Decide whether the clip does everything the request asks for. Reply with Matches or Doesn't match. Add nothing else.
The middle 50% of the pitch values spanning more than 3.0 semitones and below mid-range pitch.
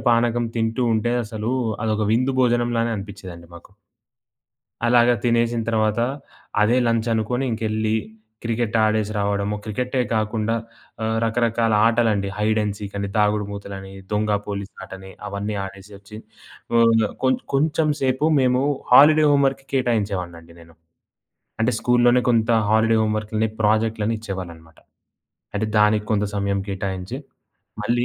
Doesn't match